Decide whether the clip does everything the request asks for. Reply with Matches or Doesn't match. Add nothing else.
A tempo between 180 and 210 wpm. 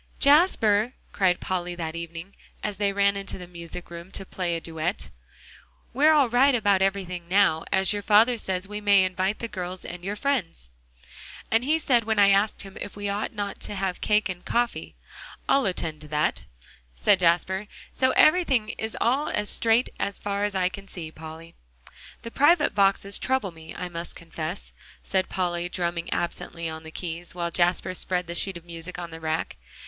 Matches